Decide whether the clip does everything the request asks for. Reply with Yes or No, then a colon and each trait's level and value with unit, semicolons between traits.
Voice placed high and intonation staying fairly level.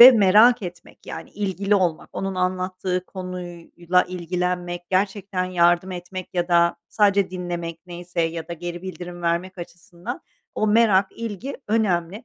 No: medium, 180 Hz; narrow, 1.9 semitones